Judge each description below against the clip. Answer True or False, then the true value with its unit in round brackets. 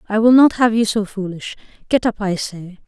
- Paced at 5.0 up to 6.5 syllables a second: True (5.4 syllables/s)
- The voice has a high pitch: True (210 Hz)